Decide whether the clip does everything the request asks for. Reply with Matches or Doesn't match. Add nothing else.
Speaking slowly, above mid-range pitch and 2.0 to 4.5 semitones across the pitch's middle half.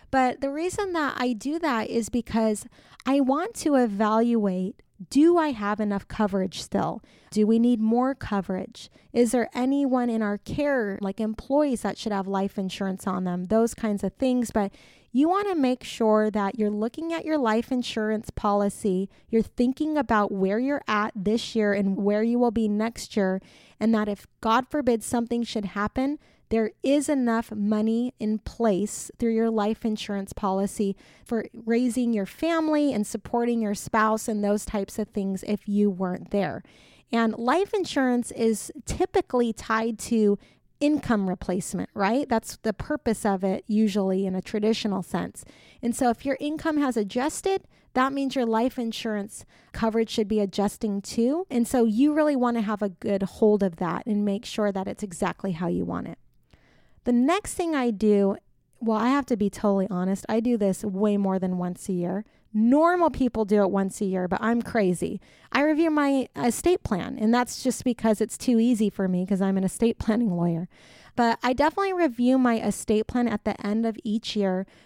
Doesn't match